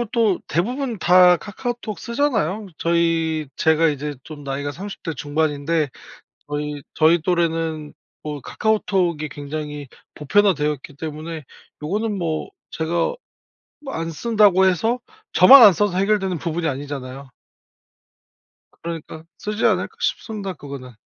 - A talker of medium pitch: Yes, medium, 165 Hz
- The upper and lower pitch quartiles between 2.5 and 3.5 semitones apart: No, average, 5.1 semitones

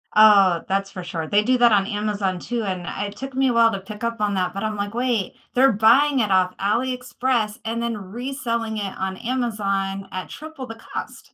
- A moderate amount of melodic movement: Yes, average, 3.5 semitones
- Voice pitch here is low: No, high, 215 Hz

